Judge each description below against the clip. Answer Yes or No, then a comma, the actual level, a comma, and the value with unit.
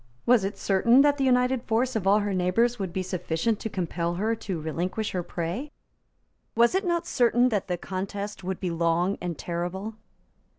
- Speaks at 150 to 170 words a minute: No, average, 185 wpm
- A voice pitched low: No, high, 200 Hz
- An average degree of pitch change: Yes, average, 4.9 semitones